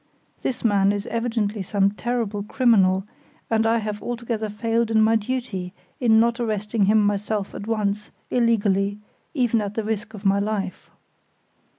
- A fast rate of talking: No, average, 155 wpm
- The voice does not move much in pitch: Yes, narrow, 2.2 semitones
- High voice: Yes, high, 215 Hz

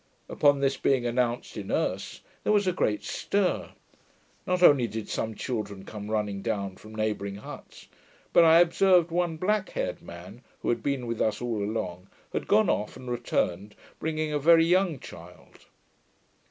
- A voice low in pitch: Yes, low, 120 Hz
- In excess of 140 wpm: Yes, average, 165 wpm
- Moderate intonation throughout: No, wide, 7.8 semitones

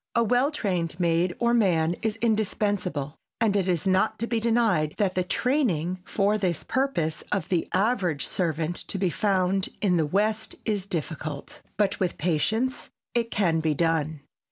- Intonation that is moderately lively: Yes, average, 4.7 semitones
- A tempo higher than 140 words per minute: Yes, average, 165 wpm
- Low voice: No, high, 190 Hz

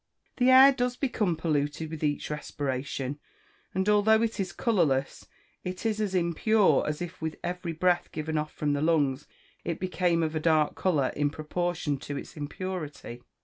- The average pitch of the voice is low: No, medium, 165 Hz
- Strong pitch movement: No, average, 4.1 semitones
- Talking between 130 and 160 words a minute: No, average, 170 wpm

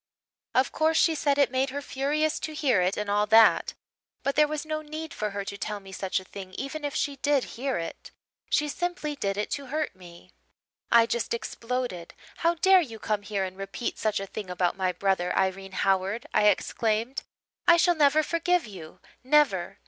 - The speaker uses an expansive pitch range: Yes, wide, 7.2 semitones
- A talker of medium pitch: No, high, 235 Hz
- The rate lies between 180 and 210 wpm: Yes, average, 200 wpm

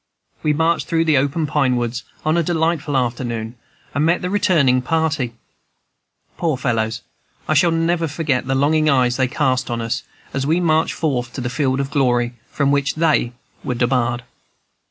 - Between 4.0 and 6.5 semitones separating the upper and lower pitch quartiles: Yes, average, 4.3 semitones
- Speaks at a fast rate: No, average, 175 wpm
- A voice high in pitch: No, medium, 140 Hz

